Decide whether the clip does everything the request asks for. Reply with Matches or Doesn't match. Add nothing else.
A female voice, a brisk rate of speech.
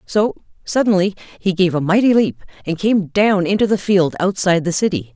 Doesn't match